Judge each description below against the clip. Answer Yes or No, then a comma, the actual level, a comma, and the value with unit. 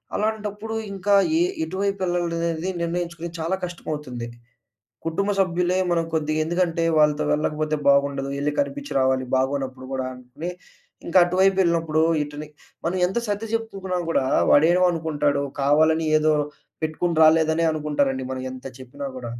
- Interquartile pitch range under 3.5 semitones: No, average, 3.8 semitones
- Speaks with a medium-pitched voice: Yes, medium, 160 Hz